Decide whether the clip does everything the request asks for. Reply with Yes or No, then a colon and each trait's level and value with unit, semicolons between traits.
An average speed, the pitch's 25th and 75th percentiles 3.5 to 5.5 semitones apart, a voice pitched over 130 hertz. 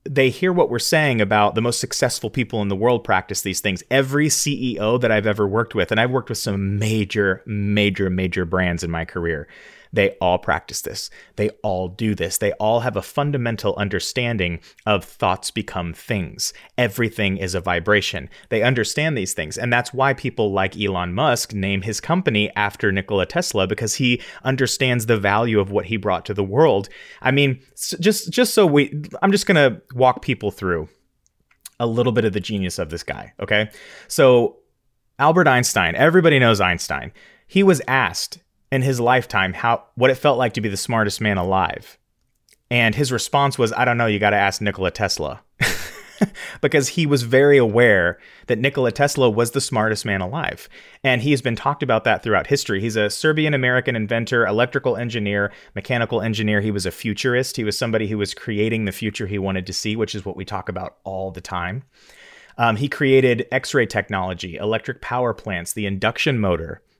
No: average, 190 wpm; average, 4.3 semitones; low, 110 Hz